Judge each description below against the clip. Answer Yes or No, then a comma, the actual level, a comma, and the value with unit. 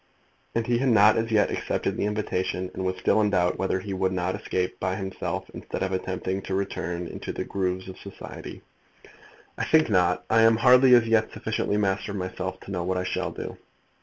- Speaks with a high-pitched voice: No, very low, 95 Hz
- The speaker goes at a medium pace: No, fast, 210 wpm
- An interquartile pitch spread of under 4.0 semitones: Yes, average, 2.7 semitones